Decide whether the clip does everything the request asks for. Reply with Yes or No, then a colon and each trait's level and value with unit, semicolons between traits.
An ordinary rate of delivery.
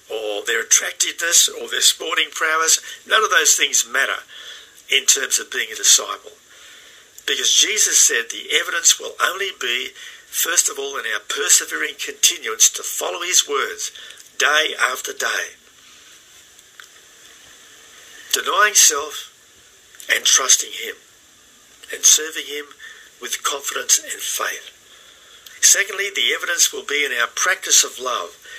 No: slow, 130 wpm